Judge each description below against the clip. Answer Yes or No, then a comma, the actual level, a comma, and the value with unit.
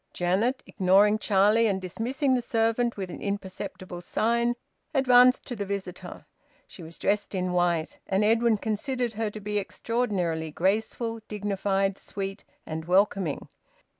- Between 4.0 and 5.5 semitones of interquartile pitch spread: No, average, 3.4 semitones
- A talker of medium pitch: No, high, 205 Hz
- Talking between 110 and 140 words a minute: Yes, slow, 135 wpm